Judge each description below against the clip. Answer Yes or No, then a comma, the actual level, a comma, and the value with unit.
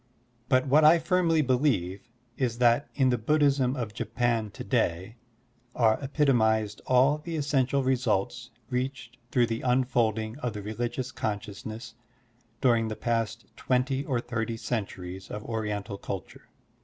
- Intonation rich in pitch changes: No, average, 3.2 semitones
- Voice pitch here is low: Yes, low, 120 Hz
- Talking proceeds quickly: No, average, 140 wpm